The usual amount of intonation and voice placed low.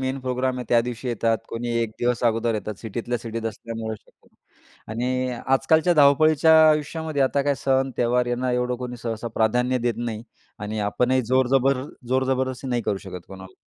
No: narrow, 2.3 semitones; low, 125 Hz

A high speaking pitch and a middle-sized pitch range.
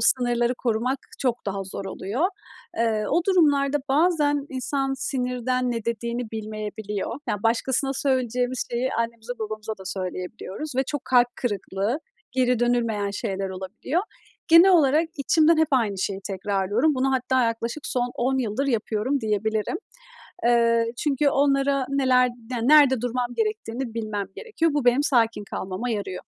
Yes: high, 245 Hz; average, 3.9 semitones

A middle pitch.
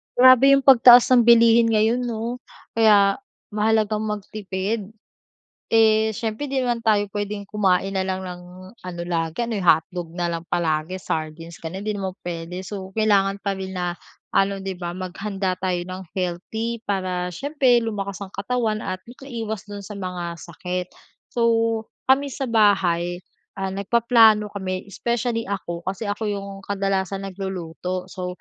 No: high, 200 Hz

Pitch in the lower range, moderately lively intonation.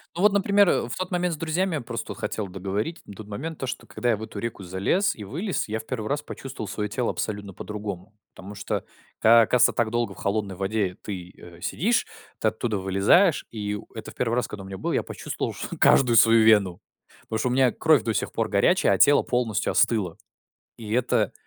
Yes: low, 110 Hz; average, 4.2 semitones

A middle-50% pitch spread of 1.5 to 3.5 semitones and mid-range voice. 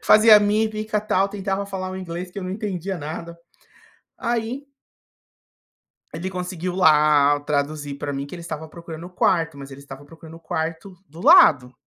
No: average, 4.4 semitones; medium, 170 Hz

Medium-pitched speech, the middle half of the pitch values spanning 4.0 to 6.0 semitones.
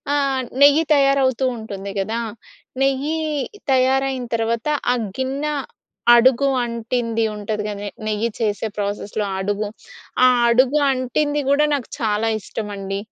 No: high, 235 Hz; average, 4.3 semitones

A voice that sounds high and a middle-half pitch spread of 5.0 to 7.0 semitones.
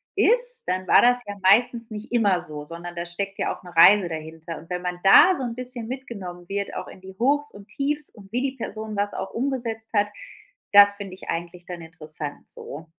Yes: high, 200 Hz; average, 5.3 semitones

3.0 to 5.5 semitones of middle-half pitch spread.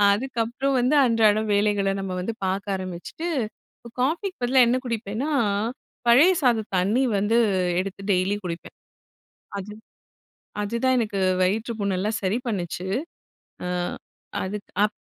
Yes: average, 3.7 semitones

